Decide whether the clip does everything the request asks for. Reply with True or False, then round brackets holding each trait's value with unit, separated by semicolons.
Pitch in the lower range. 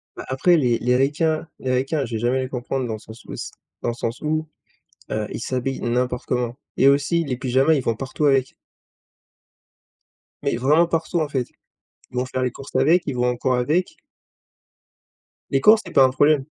True (130 Hz)